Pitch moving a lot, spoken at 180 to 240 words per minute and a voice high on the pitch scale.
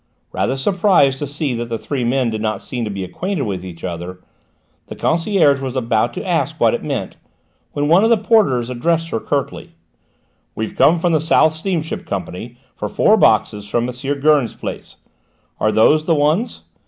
No: wide, 6.4 semitones; average, 185 wpm; low, 135 Hz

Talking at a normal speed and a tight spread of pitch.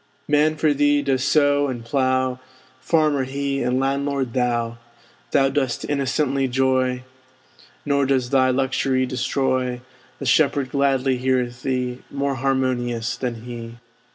No: slow, 125 wpm; narrow, 1.7 semitones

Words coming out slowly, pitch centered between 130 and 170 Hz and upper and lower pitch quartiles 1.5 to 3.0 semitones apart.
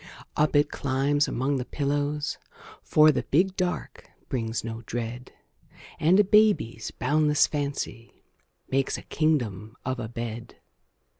No: slow, 130 wpm; medium, 140 Hz; average, 4.3 semitones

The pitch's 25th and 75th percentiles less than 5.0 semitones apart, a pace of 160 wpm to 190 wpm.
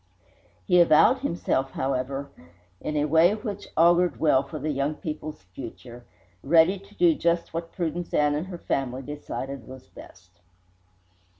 No: average, 4.2 semitones; average, 145 wpm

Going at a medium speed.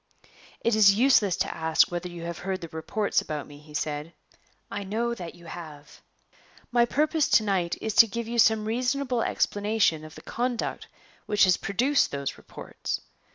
Yes: average, 175 wpm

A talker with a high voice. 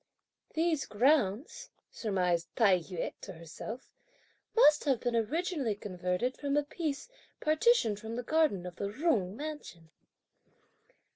Yes: high, 230 Hz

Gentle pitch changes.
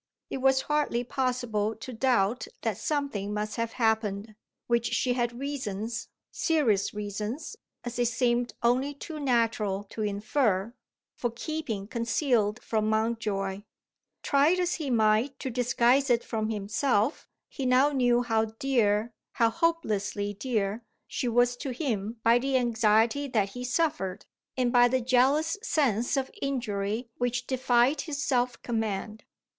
No: average, 3.4 semitones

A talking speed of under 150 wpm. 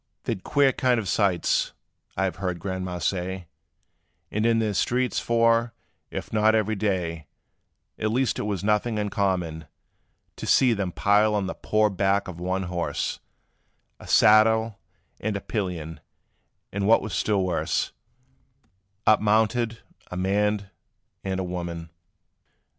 Yes: average, 140 wpm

